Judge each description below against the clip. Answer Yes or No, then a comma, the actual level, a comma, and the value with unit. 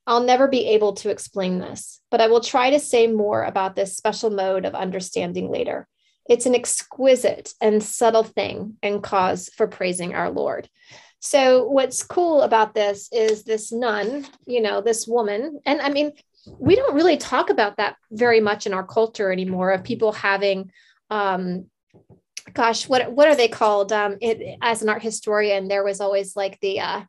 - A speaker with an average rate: Yes, average, 180 wpm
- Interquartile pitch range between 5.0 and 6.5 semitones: No, average, 3.5 semitones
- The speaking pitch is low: No, high, 220 Hz